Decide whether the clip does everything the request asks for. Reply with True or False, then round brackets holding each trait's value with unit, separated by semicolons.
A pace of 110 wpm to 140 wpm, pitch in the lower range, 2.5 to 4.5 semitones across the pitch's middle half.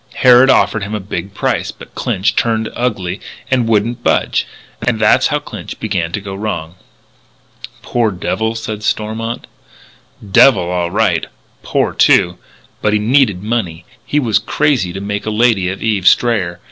False (160 wpm; 105 Hz; 3.4 semitones)